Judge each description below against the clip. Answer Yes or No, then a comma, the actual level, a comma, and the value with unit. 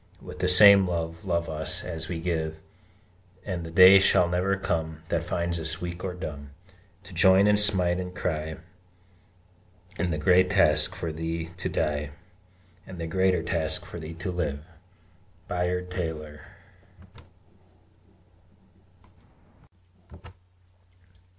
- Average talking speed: No, slow, 125 wpm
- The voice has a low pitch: Yes, very low, 85 Hz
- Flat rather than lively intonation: Yes, narrow, 2.2 semitones